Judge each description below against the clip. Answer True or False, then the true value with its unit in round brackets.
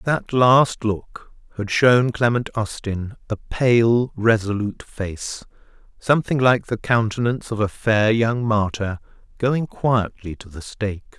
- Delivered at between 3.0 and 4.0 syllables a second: True (3.9 syllables/s)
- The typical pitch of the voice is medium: False (115 Hz)